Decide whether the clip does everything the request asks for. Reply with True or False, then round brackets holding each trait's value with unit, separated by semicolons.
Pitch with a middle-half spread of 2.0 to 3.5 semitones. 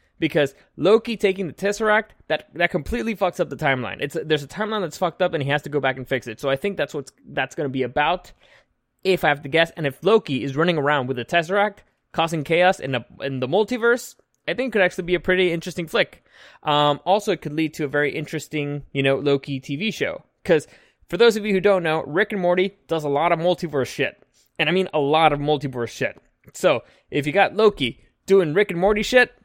False (5.2 semitones)